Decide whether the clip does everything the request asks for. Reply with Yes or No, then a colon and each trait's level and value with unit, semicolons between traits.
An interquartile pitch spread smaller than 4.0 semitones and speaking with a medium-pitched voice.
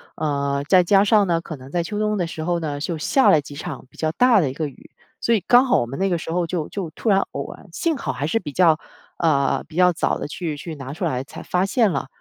No: average, 4.9 semitones; medium, 165 Hz